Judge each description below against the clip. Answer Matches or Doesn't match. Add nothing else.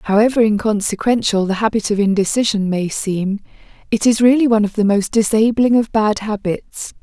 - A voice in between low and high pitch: Doesn't match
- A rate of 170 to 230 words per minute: Doesn't match